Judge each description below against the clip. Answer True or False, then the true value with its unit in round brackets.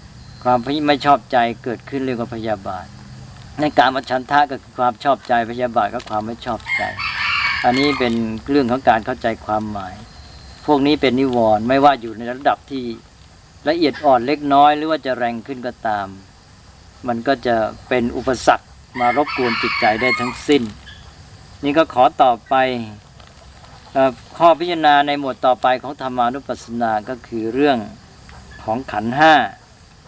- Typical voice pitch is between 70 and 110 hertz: False (125 Hz)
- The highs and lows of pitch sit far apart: False (3.3 semitones)